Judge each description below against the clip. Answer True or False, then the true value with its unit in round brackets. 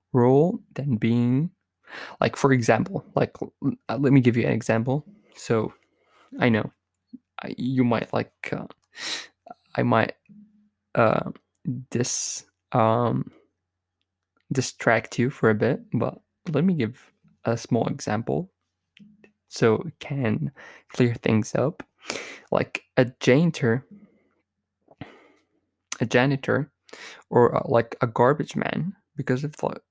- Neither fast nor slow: False (120 wpm)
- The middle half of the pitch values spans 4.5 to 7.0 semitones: True (5.1 semitones)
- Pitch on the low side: True (130 Hz)